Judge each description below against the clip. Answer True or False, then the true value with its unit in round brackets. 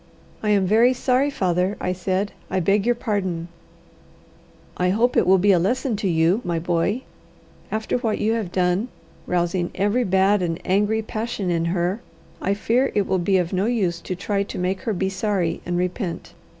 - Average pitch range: True (3.3 semitones)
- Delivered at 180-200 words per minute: True (190 wpm)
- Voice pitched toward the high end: True (195 Hz)